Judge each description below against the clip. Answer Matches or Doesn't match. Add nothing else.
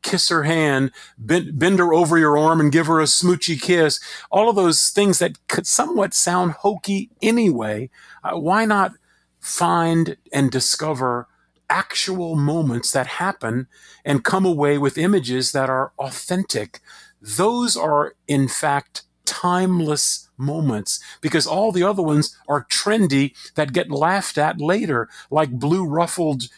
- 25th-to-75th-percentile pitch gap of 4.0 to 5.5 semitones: Matches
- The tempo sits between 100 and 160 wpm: Matches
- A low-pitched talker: Doesn't match